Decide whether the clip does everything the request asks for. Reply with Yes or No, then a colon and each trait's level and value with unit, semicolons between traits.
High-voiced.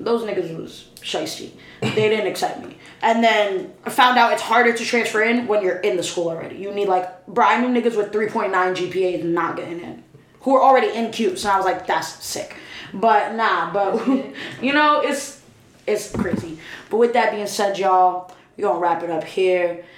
Yes: high, 205 Hz